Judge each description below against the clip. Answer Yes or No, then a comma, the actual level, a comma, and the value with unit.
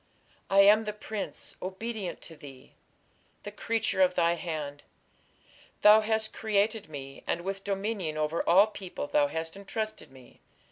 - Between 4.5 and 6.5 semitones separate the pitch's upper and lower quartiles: Yes, average, 4.9 semitones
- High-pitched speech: Yes, high, 195 Hz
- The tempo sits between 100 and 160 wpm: Yes, average, 145 wpm